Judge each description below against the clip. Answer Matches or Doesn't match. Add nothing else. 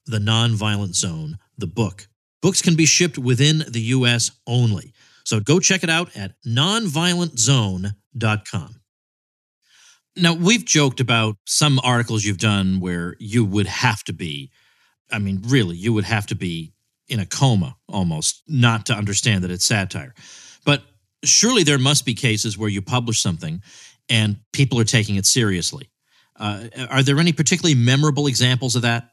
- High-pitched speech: Doesn't match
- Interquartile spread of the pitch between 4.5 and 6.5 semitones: Matches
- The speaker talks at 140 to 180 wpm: Matches